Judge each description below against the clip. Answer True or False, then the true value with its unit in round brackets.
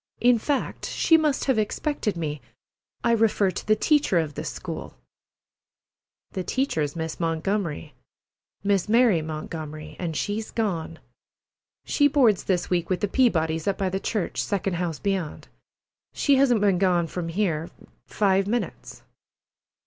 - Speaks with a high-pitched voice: True (195 Hz)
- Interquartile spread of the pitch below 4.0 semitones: False (5.1 semitones)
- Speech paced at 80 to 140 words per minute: True (135 wpm)